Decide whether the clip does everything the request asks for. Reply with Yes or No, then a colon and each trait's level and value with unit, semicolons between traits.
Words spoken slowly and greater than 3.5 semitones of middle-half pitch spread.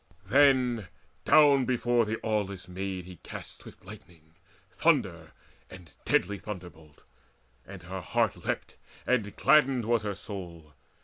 Yes: slow, 125 wpm; average, 5.2 semitones